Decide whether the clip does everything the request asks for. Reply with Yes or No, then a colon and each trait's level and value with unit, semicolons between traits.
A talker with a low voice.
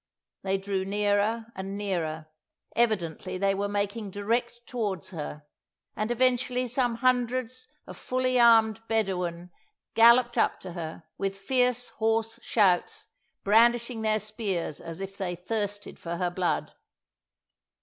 No: high, 210 Hz